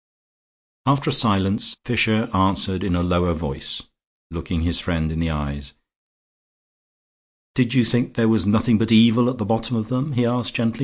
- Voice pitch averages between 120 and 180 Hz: No, low, 110 Hz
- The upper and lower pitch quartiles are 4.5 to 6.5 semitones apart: Yes, average, 5.3 semitones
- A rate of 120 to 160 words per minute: No, average, 170 wpm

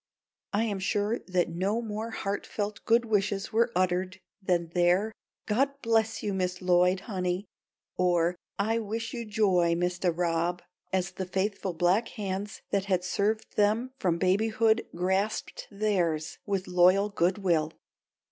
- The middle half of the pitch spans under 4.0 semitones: Yes, average, 3.1 semitones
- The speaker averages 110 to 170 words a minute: Yes, average, 140 wpm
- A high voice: Yes, high, 195 Hz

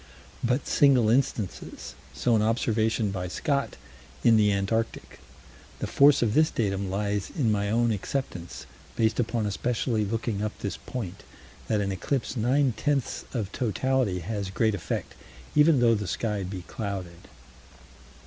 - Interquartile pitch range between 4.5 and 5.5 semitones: No, average, 3.6 semitones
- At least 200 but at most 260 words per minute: No, average, 145 wpm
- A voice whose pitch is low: Yes, low, 110 Hz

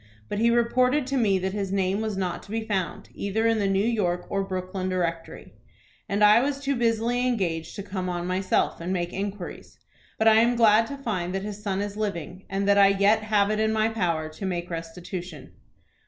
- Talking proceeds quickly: Yes, fast, 215 wpm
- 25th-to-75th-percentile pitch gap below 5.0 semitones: Yes, average, 3.2 semitones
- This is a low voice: No, high, 200 Hz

